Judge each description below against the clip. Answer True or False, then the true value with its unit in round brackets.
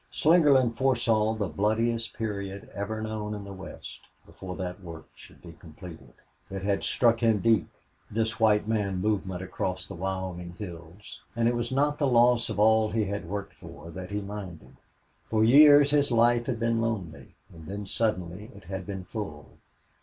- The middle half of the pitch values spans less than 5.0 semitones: True (3.6 semitones)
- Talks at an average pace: True (175 wpm)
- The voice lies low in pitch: True (105 Hz)